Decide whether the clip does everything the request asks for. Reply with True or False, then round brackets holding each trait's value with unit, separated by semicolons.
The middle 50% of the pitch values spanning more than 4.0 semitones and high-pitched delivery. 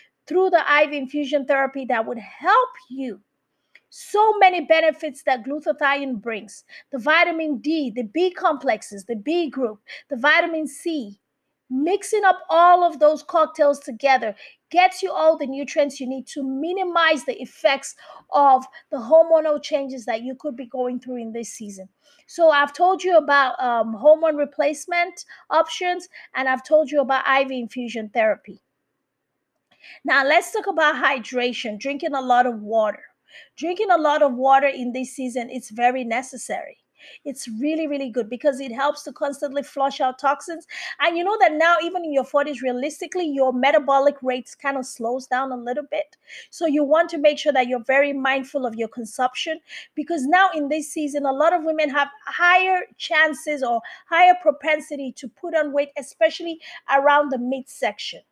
False (3.7 semitones; 285 Hz)